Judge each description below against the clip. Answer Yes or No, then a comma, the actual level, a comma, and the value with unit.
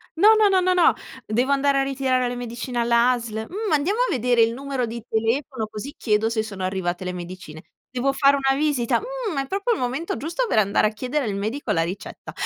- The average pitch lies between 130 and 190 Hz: No, very high, 250 Hz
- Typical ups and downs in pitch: Yes, average, 4.5 semitones